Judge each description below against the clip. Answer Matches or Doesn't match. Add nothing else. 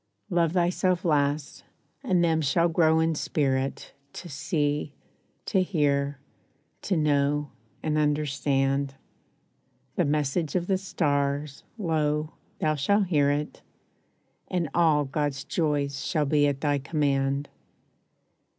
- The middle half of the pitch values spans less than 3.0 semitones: Matches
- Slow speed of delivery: Matches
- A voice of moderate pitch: Matches